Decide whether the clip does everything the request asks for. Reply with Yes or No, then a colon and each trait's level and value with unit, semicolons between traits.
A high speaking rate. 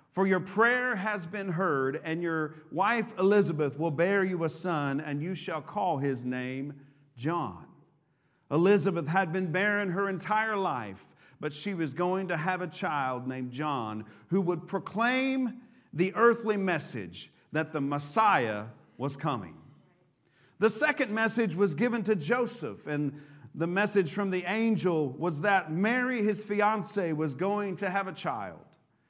No: average, 155 wpm